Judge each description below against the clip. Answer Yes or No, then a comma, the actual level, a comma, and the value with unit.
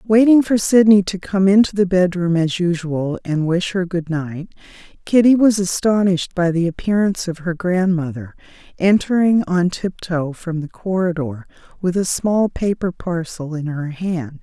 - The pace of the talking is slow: No, average, 160 wpm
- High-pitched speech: No, medium, 180 Hz